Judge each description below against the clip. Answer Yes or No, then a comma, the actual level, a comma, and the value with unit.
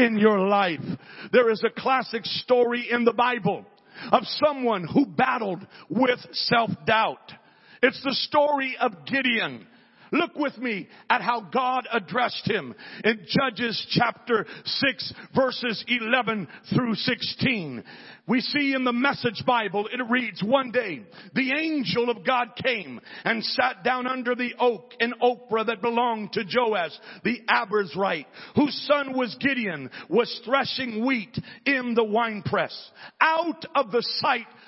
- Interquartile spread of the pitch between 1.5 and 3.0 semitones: Yes, narrow, 2.6 semitones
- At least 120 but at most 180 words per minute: Yes, average, 145 wpm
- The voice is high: Yes, high, 240 Hz